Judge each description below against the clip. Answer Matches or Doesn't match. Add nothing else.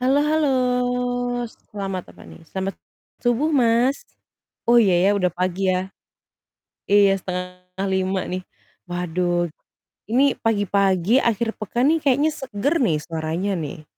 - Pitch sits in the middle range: Doesn't match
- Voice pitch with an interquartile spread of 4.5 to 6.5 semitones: Matches